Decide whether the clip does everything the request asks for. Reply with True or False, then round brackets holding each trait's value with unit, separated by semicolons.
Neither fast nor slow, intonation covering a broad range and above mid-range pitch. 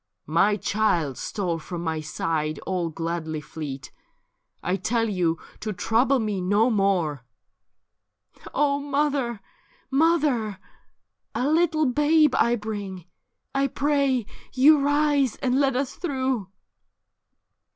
False (120 wpm; 7.8 semitones; 225 Hz)